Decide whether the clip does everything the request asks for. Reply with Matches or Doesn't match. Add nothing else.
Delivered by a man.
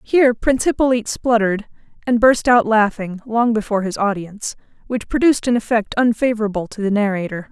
Doesn't match